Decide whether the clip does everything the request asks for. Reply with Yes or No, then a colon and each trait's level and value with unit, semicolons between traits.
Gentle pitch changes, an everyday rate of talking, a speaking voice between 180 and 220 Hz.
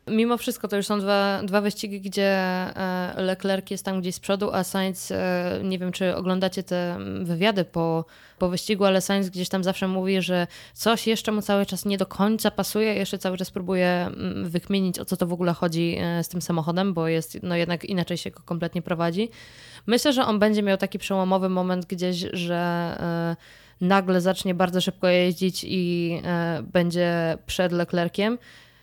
No: narrow, 2.0 semitones; fast, 175 wpm; medium, 185 Hz